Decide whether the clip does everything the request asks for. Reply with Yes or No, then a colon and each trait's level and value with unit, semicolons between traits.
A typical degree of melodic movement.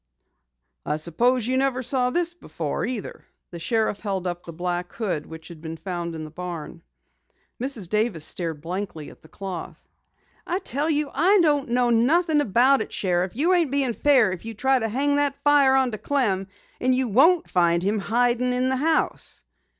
No: wide, 7.3 semitones